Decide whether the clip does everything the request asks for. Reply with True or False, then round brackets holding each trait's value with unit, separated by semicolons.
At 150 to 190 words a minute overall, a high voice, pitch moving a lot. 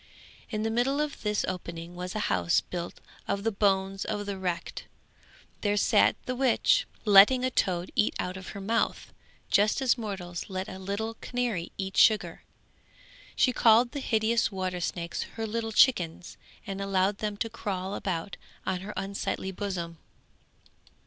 False (160 wpm; 200 Hz; 3.2 semitones)